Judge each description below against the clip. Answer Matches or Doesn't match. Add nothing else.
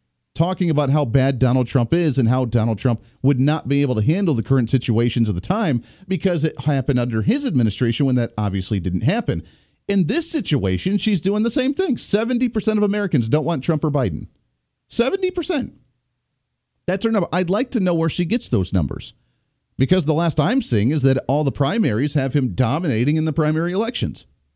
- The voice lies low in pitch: Doesn't match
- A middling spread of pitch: Doesn't match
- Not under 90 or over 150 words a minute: Doesn't match